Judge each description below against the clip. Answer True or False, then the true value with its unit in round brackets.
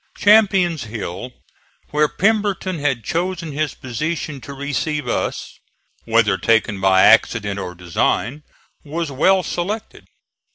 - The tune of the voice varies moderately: False (7.4 semitones)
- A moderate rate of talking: False (115 wpm)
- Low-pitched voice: False (145 Hz)